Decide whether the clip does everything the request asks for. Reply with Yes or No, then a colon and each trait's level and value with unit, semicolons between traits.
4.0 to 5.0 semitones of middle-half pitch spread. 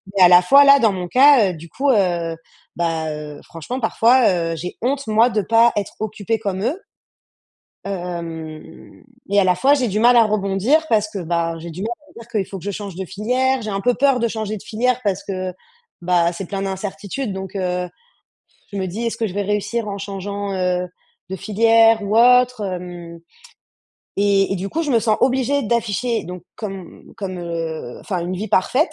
Yes: average, 4.3 semitones